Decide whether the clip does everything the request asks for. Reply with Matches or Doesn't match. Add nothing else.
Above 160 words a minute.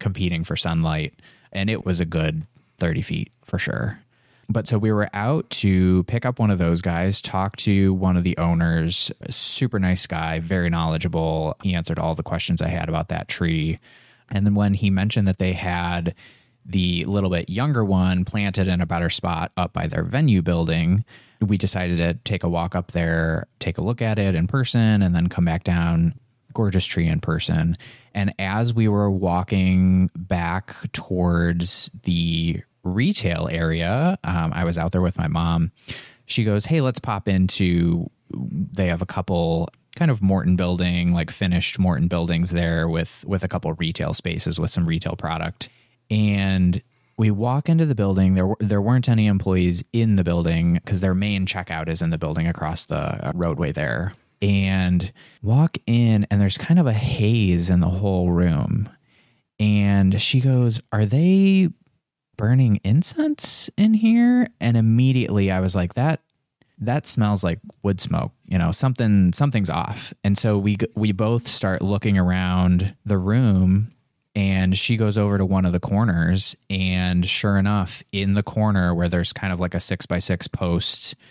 Matches